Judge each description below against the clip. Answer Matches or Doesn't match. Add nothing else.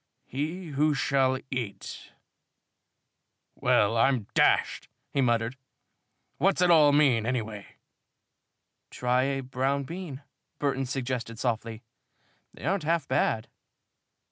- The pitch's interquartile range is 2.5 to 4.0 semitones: Matches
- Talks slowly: Matches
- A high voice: Doesn't match